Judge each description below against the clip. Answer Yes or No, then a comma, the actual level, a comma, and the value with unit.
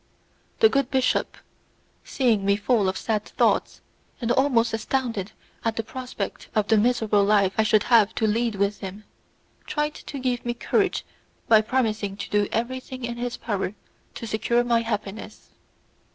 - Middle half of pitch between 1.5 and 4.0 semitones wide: Yes, average, 2.8 semitones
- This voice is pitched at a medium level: No, high, 225 Hz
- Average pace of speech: Yes, average, 160 wpm